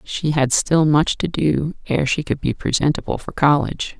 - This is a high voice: No, medium, 145 Hz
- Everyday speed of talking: Yes, average, 195 wpm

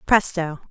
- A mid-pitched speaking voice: Yes, medium, 175 Hz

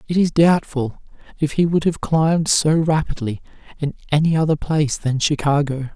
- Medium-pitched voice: Yes, medium, 150 Hz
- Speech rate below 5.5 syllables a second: Yes, 5.1 syllables/s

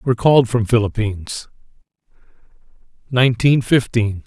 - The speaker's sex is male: Yes, male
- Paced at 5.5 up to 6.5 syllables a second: No, 5.0 syllables/s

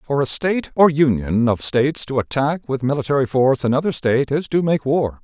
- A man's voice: Yes, male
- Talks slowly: No, fast, 205 wpm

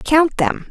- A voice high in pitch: Yes, very high, 325 Hz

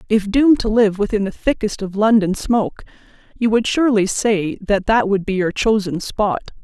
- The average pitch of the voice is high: Yes, high, 210 Hz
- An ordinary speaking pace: Yes, average, 190 wpm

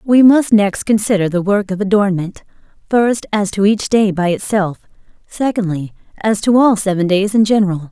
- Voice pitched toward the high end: Yes, high, 205 Hz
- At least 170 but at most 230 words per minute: Yes, average, 175 wpm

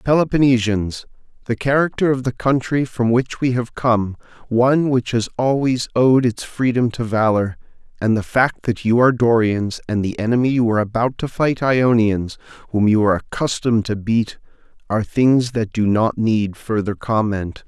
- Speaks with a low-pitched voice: Yes, low, 115 Hz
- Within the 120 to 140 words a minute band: No, average, 170 wpm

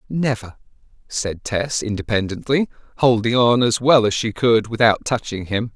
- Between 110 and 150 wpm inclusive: Yes, average, 145 wpm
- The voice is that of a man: Yes, male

